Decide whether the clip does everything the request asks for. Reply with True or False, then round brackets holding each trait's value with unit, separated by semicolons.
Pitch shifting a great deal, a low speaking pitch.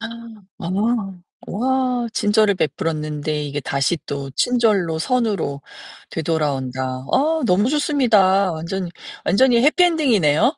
False (7.3 semitones; 200 Hz)